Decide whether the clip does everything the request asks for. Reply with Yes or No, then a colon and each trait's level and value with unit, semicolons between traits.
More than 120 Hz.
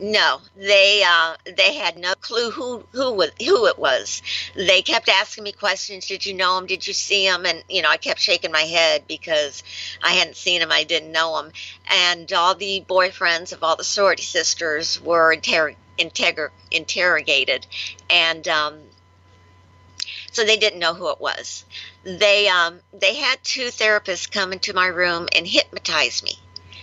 Yes: medium, 185 Hz